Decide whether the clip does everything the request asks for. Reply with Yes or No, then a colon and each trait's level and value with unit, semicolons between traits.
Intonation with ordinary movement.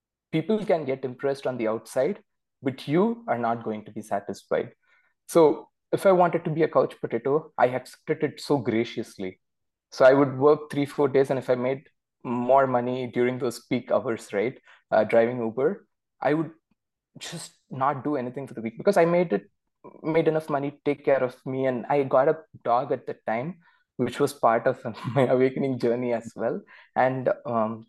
Yes: average, 3.8 semitones